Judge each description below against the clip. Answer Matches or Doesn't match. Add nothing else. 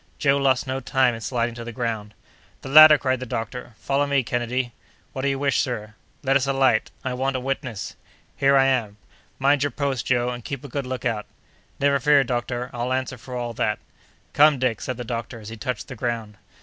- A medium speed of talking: Doesn't match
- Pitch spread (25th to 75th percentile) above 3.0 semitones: Doesn't match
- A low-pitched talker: Matches